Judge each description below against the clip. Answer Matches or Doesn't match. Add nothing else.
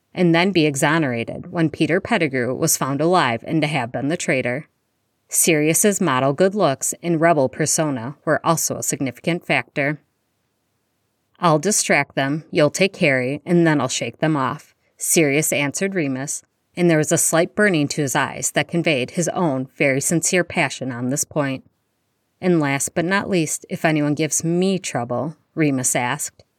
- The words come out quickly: Doesn't match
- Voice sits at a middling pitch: Matches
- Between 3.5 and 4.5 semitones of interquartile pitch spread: Matches